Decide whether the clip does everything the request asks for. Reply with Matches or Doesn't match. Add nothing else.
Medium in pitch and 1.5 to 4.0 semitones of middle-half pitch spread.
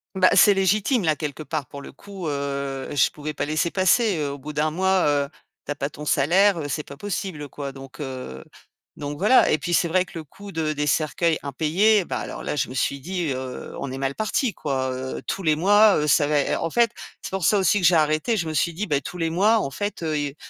Doesn't match